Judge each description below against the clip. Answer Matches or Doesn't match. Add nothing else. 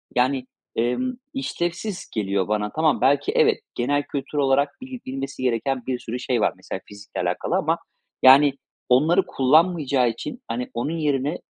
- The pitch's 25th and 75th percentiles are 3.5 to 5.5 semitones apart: Matches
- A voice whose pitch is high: Doesn't match